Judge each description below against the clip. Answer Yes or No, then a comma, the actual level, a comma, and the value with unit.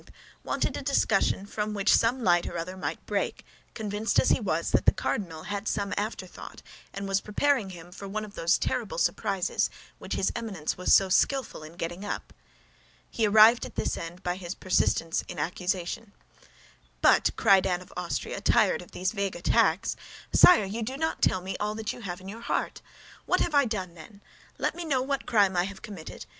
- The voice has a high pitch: Yes, high, 200 Hz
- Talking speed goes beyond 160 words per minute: Yes, average, 200 wpm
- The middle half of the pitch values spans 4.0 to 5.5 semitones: No, average, 3.4 semitones